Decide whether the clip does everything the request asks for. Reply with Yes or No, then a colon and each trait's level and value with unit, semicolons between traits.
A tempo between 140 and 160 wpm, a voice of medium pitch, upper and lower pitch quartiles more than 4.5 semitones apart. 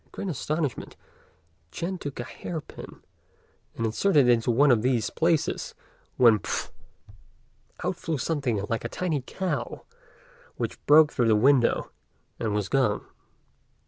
No: average, 145 wpm; low, 130 Hz; wide, 5.4 semitones